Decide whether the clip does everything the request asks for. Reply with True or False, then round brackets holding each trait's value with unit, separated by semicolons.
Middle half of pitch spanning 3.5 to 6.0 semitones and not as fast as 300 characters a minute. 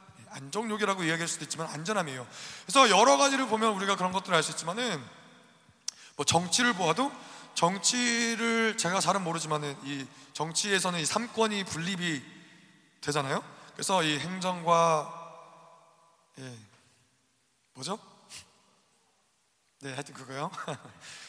True (5.2 semitones; 275 characters per minute)